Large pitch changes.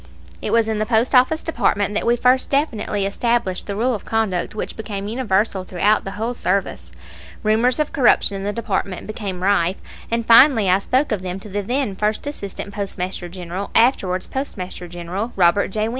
No: average, 3.5 semitones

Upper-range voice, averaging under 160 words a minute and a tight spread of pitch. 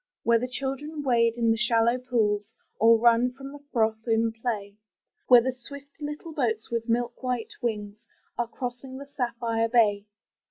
No: high, 235 Hz; average, 165 wpm; narrow, 2.2 semitones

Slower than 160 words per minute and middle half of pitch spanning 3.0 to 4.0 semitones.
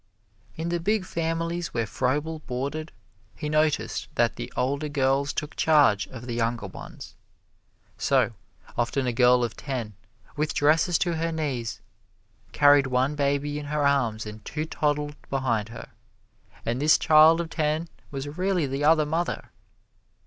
Yes: average, 150 wpm; average, 3.7 semitones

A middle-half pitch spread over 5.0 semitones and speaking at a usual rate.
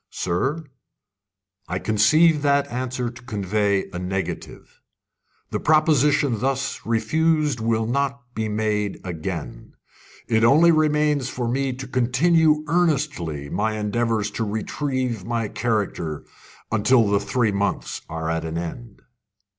No: wide, 5.4 semitones; slow, 125 wpm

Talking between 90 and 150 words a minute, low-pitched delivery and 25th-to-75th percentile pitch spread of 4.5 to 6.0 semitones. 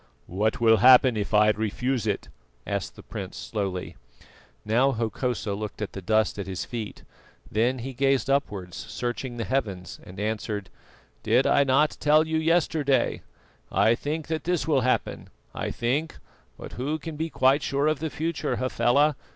No: average, 165 wpm; low, 125 Hz; average, 5.1 semitones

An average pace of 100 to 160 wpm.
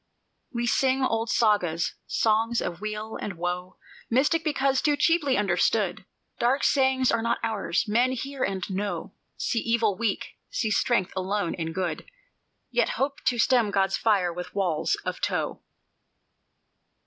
Yes: average, 145 wpm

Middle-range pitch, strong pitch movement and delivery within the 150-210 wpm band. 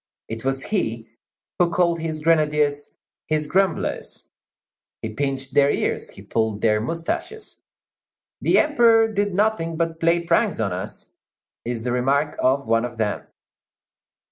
No: medium, 150 Hz; wide, 5.8 semitones; average, 140 wpm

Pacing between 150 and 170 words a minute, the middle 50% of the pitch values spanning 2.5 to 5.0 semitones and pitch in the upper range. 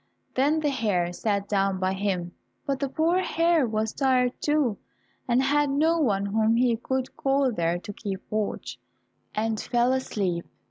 No: average, 165 wpm; wide, 5.4 semitones; high, 235 Hz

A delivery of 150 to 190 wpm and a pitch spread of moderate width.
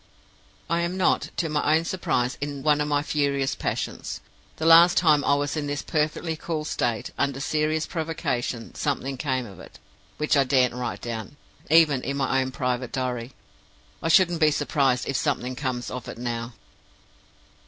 Yes: average, 175 wpm; average, 3.4 semitones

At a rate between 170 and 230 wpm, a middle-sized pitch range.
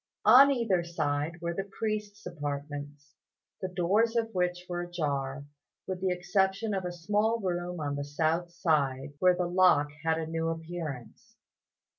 No: average, 155 wpm; average, 4.0 semitones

